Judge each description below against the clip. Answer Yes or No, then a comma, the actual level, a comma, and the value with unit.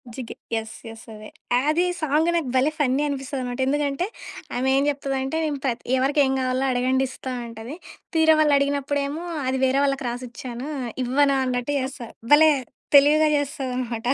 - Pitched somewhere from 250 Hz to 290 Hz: Yes, very high, 270 Hz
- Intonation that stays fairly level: Yes, narrow, 2.3 semitones